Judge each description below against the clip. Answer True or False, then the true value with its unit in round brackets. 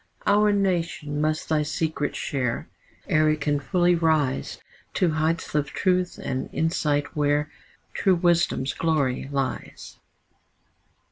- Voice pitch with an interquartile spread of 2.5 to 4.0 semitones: True (2.8 semitones)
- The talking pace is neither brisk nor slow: False (120 wpm)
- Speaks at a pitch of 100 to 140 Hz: False (155 Hz)